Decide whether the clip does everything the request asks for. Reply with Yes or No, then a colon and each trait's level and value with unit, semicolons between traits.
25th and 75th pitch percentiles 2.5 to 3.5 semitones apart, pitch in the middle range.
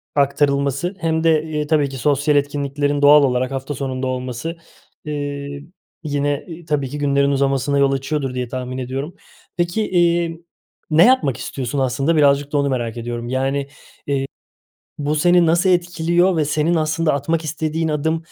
Yes: average, 2.8 semitones; medium, 145 Hz